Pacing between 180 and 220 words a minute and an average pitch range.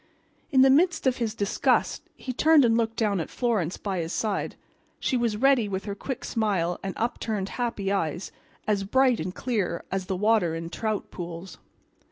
Yes: average, 185 wpm; average, 4.2 semitones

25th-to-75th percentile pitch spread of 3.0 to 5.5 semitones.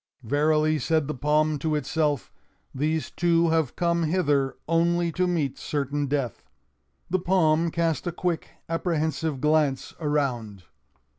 No: narrow, 2.4 semitones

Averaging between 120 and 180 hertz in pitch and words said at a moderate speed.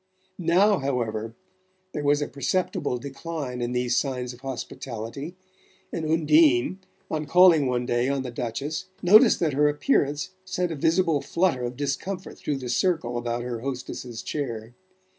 Yes: medium, 140 Hz; average, 150 wpm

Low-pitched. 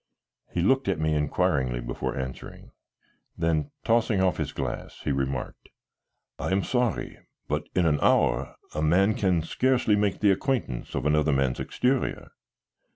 Yes: very low, 85 Hz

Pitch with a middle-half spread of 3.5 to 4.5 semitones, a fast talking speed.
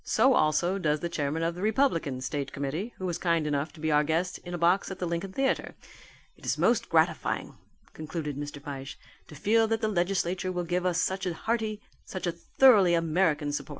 Yes: average, 3.8 semitones; fast, 210 wpm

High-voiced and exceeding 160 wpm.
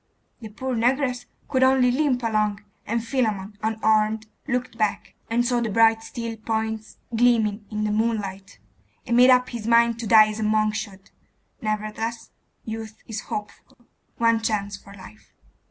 No: high, 225 Hz; average, 155 wpm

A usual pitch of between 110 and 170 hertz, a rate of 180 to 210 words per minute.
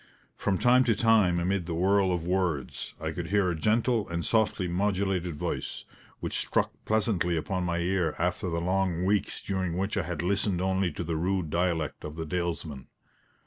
No: very low, 90 Hz; average, 185 wpm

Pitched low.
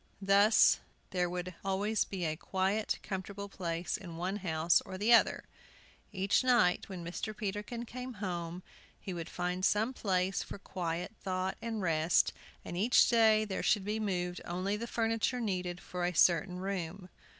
No: high, 190 Hz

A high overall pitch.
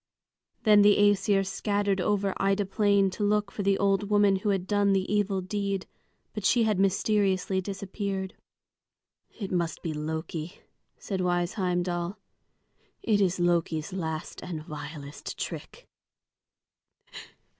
Yes: high, 195 Hz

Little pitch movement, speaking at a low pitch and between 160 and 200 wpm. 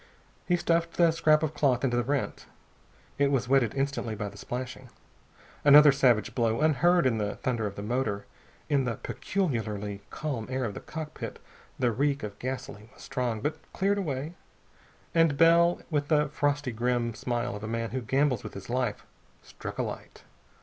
No: average, 4.4 semitones; low, 130 Hz; average, 175 wpm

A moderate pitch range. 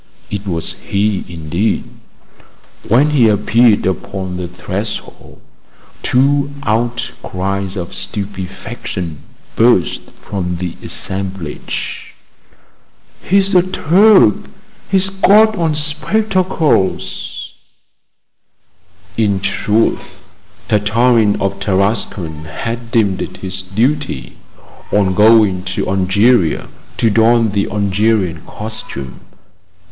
Yes: average, 4.4 semitones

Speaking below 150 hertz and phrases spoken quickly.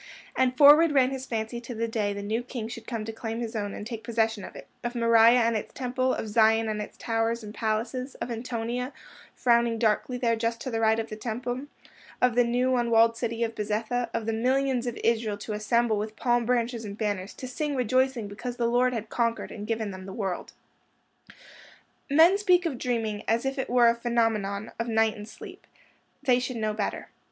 No: high, 230 Hz; fast, 210 wpm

